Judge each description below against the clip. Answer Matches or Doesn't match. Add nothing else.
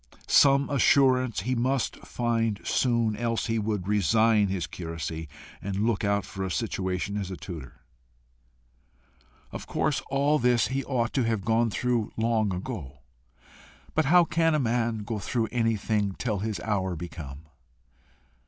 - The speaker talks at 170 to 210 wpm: Doesn't match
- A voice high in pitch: Doesn't match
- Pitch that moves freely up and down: Doesn't match